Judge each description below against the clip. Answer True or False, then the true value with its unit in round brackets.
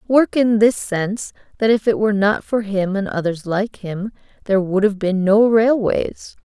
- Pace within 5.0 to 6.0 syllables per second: False (4.5 syllables/s)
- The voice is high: True (205 Hz)